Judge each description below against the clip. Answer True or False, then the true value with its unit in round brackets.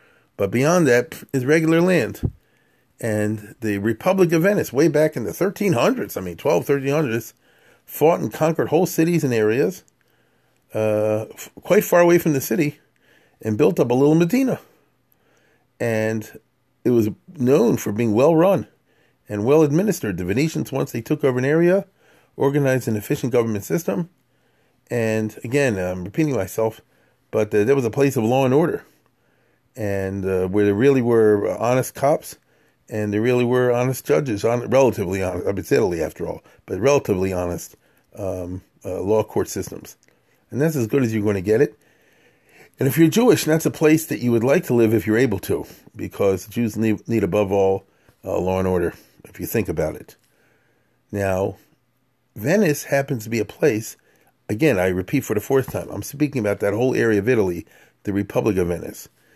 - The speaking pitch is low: True (120 Hz)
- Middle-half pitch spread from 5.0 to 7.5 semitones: True (5.6 semitones)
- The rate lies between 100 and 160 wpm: False (180 wpm)